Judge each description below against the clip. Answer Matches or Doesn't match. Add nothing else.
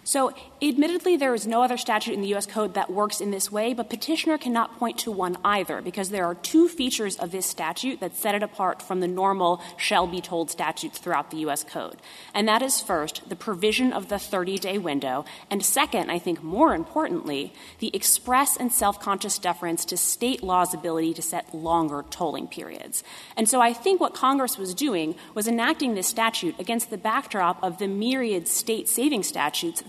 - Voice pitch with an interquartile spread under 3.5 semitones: Doesn't match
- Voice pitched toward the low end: Doesn't match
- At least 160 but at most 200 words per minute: Matches